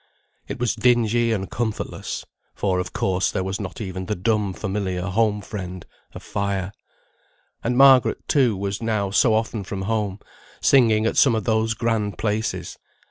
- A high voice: No, low, 105 Hz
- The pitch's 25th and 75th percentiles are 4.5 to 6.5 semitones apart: No, average, 2.8 semitones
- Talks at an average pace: Yes, average, 160 wpm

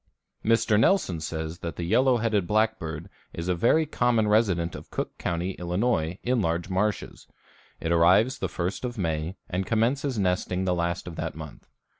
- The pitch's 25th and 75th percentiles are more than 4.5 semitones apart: Yes, average, 5.0 semitones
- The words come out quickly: No, average, 170 wpm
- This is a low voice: Yes, very low, 95 Hz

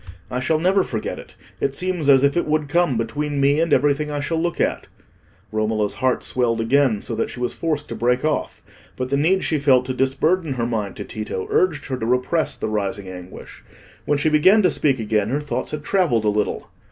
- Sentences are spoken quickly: Yes, fast, 220 wpm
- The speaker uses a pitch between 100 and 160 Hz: Yes, medium, 140 Hz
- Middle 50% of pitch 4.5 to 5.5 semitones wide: Yes, average, 4.9 semitones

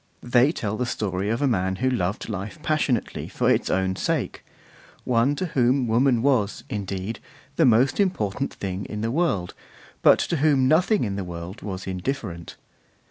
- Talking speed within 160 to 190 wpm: Yes, average, 170 wpm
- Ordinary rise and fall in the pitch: No, wide, 5.8 semitones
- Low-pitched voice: Yes, low, 115 Hz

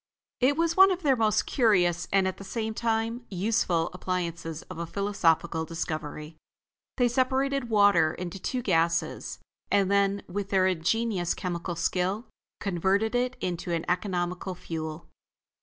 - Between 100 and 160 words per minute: Yes, average, 145 wpm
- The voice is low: No, high, 190 Hz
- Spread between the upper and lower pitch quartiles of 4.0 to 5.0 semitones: Yes, average, 4.7 semitones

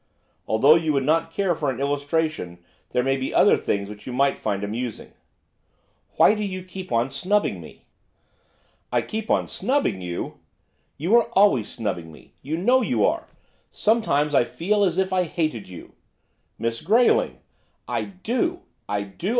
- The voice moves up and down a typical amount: No, wide, 8.8 semitones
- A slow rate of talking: No, average, 165 wpm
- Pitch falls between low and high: Yes, medium, 155 Hz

